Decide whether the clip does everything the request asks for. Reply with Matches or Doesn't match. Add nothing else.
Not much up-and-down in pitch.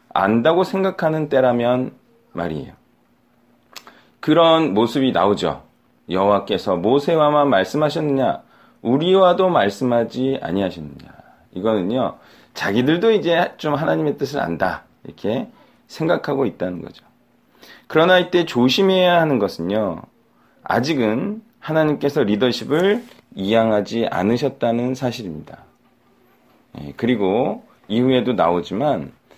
Doesn't match